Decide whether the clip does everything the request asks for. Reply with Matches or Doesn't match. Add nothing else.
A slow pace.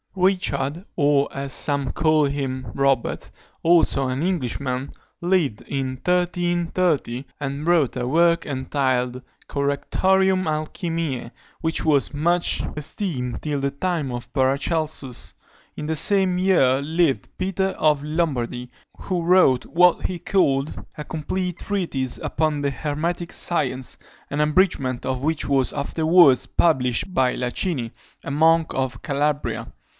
Matches